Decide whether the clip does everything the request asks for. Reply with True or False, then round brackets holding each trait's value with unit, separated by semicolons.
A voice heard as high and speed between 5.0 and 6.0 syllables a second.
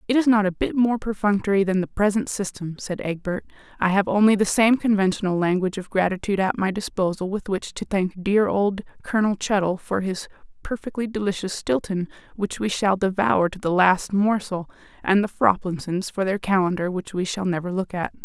True (195 Hz; 5.5 syllables/s)